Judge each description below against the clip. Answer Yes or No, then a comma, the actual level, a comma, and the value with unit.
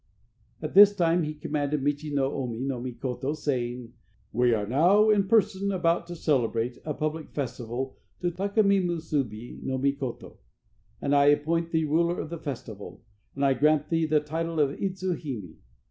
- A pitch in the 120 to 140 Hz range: No, medium, 150 Hz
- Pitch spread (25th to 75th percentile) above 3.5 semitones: Yes, average, 4.3 semitones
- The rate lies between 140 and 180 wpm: Yes, average, 170 wpm